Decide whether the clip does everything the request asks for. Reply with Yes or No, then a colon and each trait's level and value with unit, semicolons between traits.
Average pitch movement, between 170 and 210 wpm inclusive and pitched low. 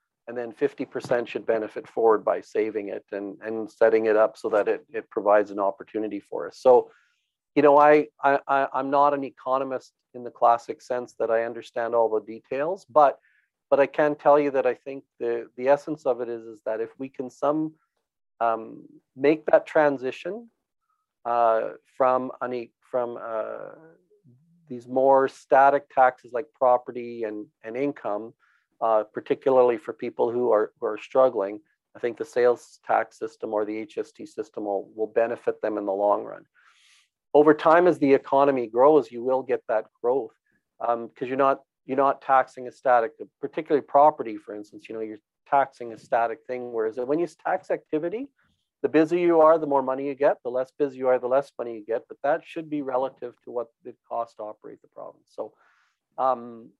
Yes: average, 4.3 semitones; average, 190 wpm; low, 130 Hz